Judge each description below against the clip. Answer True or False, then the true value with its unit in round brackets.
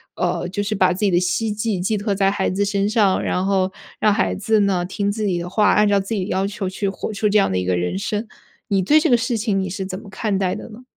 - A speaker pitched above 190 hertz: True (200 Hz)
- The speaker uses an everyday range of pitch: False (2.1 semitones)